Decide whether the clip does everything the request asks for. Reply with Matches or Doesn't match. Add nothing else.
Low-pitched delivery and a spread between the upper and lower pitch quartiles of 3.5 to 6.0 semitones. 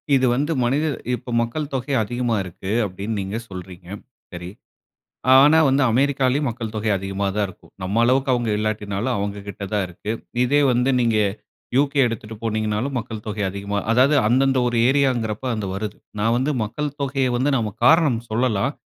Matches